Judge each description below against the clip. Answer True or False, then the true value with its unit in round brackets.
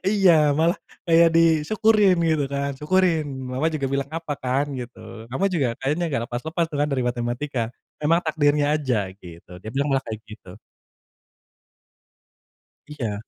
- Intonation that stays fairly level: False (4.8 semitones)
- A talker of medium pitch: True (145 Hz)